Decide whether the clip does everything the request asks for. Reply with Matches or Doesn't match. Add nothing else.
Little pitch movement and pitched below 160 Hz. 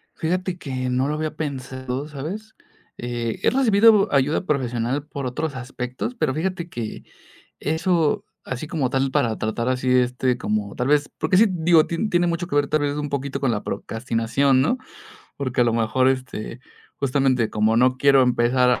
Doesn't match